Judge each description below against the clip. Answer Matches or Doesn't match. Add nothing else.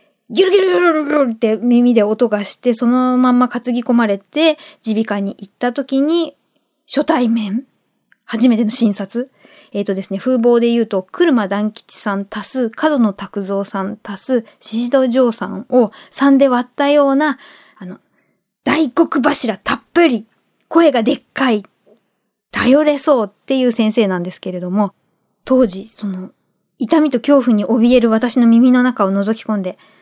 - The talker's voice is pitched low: Doesn't match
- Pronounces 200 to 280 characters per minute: Doesn't match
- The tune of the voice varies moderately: Matches